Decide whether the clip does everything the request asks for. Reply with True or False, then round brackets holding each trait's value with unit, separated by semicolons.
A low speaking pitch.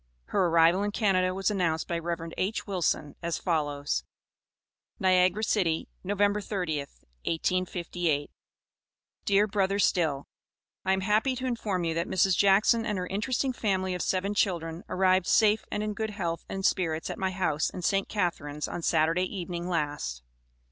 False (185 Hz)